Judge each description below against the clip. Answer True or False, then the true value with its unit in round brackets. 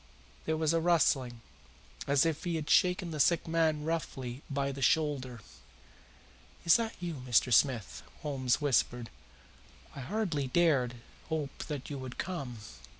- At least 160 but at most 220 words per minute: False (145 wpm)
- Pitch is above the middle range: False (145 Hz)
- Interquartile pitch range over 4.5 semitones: False (4.1 semitones)